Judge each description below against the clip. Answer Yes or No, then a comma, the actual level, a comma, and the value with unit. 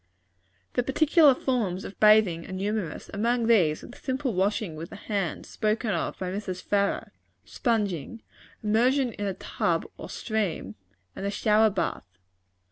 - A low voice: No, high, 210 Hz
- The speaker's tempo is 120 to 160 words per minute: Yes, average, 150 wpm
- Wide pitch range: No, average, 3.7 semitones